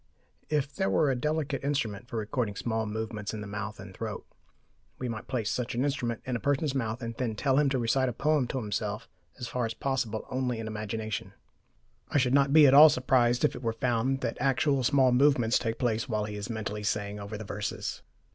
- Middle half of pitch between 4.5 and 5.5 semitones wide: No, average, 3.6 semitones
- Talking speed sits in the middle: No, fast, 220 wpm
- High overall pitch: No, low, 120 Hz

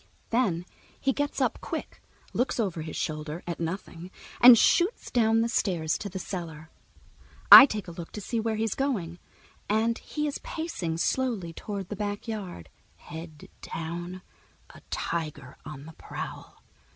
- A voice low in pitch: No, high, 190 Hz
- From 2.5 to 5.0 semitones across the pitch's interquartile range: No, wide, 5.5 semitones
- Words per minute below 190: Yes, average, 150 wpm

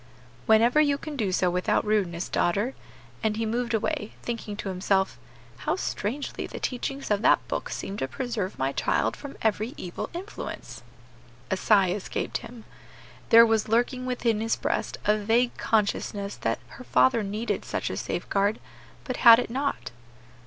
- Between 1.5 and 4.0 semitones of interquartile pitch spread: Yes, average, 3.5 semitones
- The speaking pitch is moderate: No, high, 220 Hz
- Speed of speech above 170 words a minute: No, average, 160 wpm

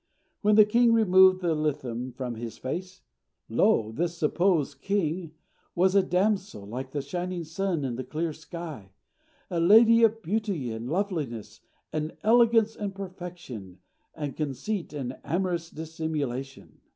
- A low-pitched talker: No, medium, 165 Hz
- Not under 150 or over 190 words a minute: No, average, 140 wpm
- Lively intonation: Yes, wide, 6.1 semitones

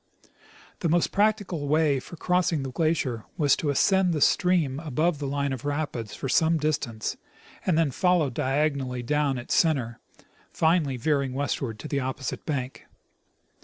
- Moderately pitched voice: Yes, medium, 145 Hz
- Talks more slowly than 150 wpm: No, average, 155 wpm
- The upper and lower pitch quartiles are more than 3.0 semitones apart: Yes, average, 3.5 semitones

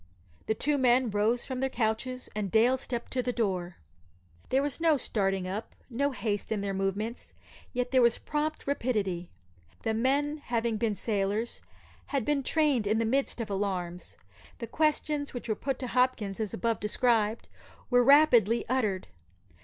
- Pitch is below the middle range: No, high, 235 Hz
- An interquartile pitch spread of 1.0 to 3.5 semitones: No, average, 3.9 semitones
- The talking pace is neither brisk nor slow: Yes, average, 165 wpm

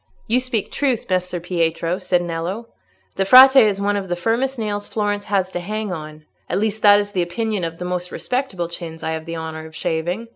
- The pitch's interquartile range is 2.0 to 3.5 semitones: No, average, 3.9 semitones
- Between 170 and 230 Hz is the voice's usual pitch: Yes, high, 190 Hz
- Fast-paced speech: Yes, fast, 210 wpm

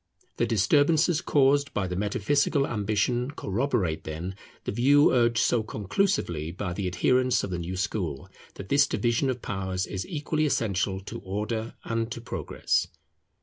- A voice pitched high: No, low, 110 Hz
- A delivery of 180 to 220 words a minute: No, average, 145 wpm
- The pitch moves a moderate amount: No, wide, 6.0 semitones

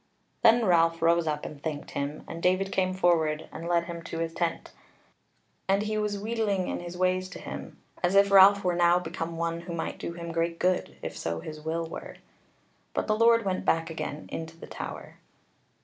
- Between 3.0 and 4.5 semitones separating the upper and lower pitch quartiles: No, narrow, 2.5 semitones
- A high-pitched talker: No, medium, 170 Hz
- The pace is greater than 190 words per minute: Yes, average, 200 wpm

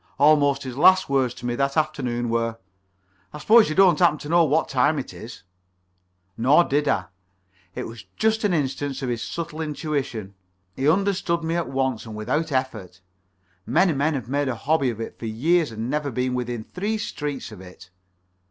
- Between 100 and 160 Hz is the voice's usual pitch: Yes, medium, 140 Hz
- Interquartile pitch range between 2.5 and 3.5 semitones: No, average, 4.9 semitones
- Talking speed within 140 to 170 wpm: No, average, 190 wpm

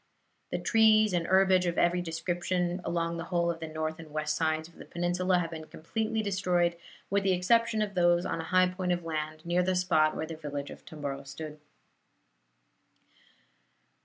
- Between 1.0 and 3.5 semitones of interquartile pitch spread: Yes, narrow, 2.6 semitones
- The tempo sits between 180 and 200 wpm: Yes, average, 185 wpm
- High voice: No, medium, 175 Hz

